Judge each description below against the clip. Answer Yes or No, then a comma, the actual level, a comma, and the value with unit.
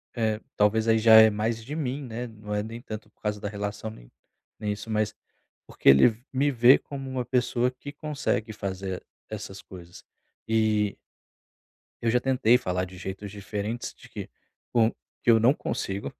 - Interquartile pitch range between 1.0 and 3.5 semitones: Yes, average, 2.9 semitones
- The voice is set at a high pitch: No, low, 110 Hz